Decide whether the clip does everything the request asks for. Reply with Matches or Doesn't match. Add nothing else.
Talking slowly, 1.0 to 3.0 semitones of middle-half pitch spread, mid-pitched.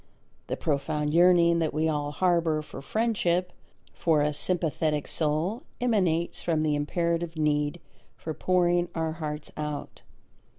Matches